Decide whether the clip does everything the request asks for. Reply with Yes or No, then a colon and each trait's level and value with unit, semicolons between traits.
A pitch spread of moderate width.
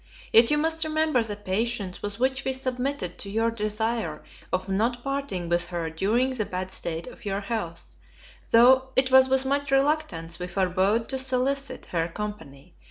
No: wide, 6.0 semitones